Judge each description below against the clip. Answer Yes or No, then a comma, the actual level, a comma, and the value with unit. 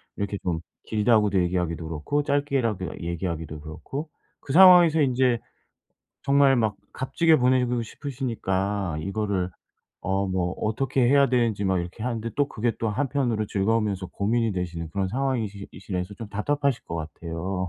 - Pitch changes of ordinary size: No, wide, 5.8 semitones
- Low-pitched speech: Yes, low, 105 Hz